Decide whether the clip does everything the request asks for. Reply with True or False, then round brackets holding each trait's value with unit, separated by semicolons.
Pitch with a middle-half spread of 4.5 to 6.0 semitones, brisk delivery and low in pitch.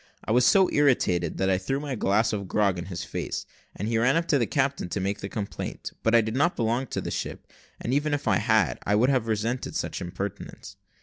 True (5.0 semitones; 240 wpm; 110 Hz)